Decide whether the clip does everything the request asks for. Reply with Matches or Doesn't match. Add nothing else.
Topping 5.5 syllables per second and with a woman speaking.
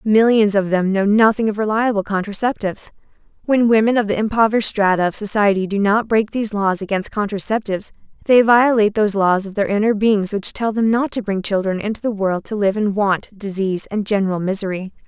Matches